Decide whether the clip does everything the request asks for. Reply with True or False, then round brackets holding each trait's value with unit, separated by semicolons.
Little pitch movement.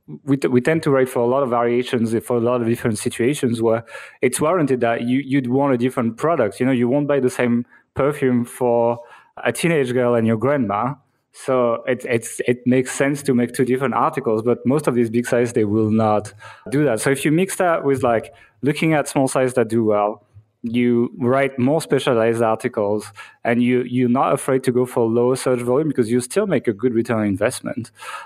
True (2.3 semitones)